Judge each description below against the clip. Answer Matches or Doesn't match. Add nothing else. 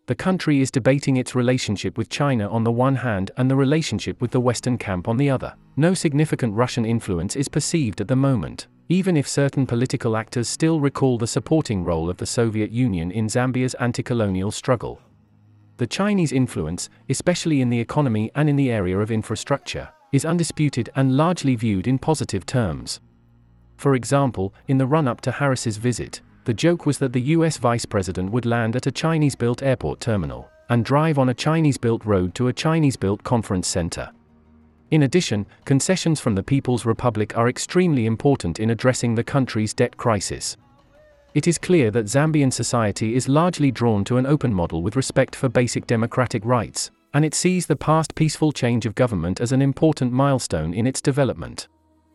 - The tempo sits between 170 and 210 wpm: Matches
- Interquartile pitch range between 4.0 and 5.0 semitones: Matches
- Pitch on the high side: Doesn't match